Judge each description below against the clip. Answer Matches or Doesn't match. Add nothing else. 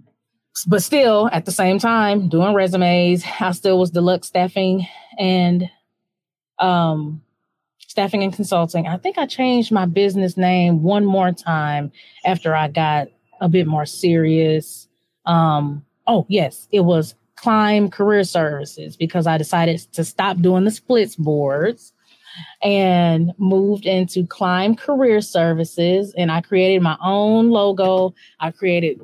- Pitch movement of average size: Matches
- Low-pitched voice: Doesn't match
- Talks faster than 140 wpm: Doesn't match